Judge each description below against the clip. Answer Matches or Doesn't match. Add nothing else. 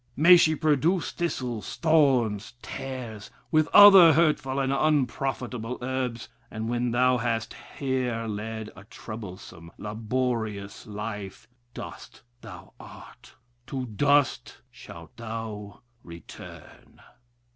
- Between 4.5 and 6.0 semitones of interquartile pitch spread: Doesn't match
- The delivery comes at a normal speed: Doesn't match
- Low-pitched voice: Matches